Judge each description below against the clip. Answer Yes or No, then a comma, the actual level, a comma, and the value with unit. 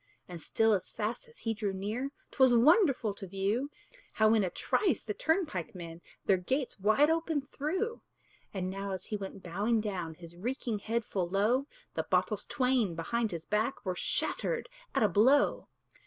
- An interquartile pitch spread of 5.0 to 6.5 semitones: Yes, wide, 5.6 semitones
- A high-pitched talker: Yes, high, 215 Hz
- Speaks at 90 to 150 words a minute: No, average, 175 wpm